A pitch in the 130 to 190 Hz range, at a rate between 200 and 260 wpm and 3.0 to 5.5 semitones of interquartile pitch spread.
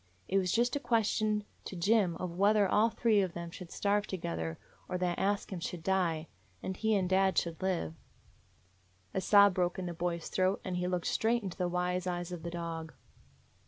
No: medium, 185 Hz; fast, 205 wpm; narrow, 2.6 semitones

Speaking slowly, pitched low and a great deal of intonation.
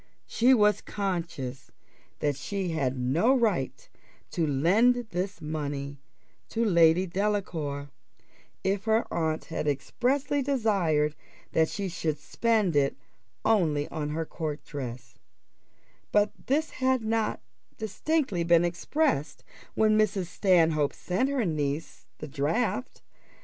No: slow, 120 wpm; medium, 175 Hz; wide, 6.6 semitones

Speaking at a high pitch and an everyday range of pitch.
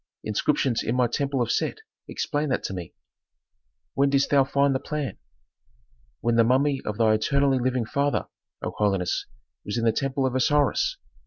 No: low, 130 Hz; average, 3.5 semitones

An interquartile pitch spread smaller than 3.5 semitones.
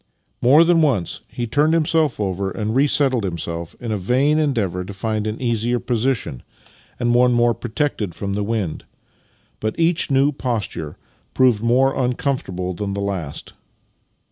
No: average, 5.1 semitones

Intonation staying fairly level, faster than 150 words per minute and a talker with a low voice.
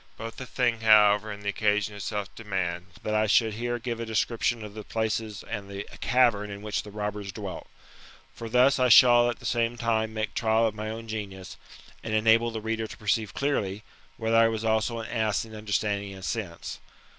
Yes: narrow, 1.8 semitones; fast, 205 wpm; low, 110 Hz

